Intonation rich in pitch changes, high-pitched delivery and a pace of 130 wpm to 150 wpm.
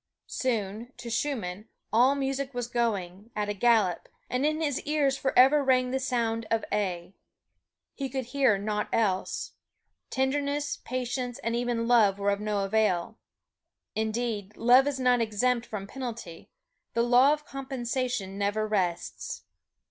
No: average, 3.9 semitones; high, 235 Hz; average, 140 wpm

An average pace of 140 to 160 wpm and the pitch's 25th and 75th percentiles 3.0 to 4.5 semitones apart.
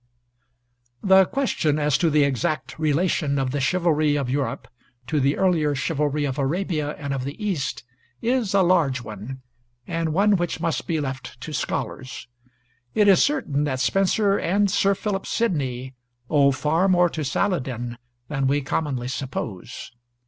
No: average, 155 wpm; average, 5.1 semitones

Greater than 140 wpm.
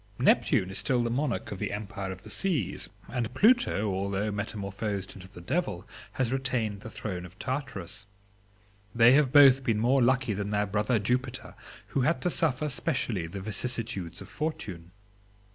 Yes: average, 165 wpm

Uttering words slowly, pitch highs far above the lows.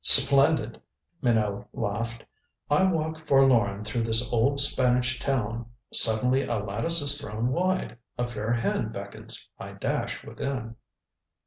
No: slow, 125 wpm; average, 3.6 semitones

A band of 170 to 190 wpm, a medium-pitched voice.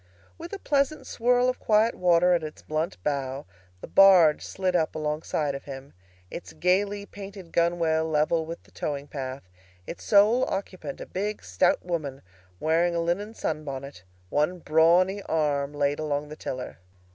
No: average, 160 wpm; medium, 165 Hz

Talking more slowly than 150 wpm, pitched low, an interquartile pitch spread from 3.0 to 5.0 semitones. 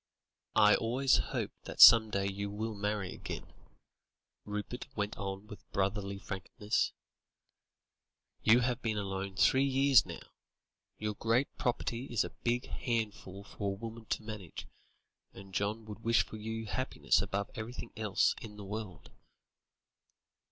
No: average, 140 wpm; low, 105 Hz; narrow, 2.4 semitones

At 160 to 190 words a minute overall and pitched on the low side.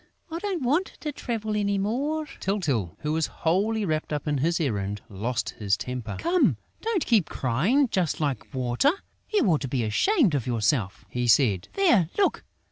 No: average, 180 wpm; medium, 160 Hz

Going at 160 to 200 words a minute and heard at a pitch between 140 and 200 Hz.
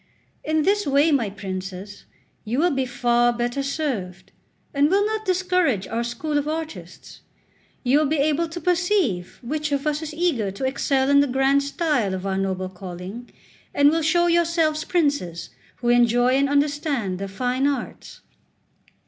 No: average, 165 wpm; very high, 275 Hz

